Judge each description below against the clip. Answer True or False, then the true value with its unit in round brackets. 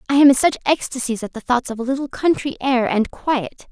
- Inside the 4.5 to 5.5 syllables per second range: False (5.7 syllables/s)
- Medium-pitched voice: False (255 Hz)